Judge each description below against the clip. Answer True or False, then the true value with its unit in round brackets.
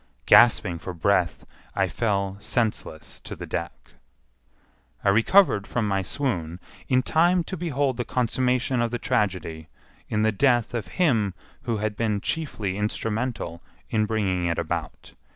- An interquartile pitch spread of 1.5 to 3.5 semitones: False (4.3 semitones)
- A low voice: True (110 Hz)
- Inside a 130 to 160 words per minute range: True (145 wpm)